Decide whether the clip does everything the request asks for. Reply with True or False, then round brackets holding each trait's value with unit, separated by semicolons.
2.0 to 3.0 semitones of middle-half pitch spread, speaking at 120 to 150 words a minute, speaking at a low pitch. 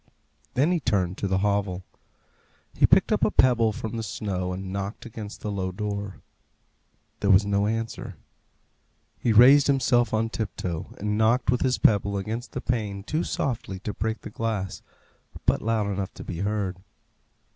False (2.5 semitones; 165 wpm; 105 Hz)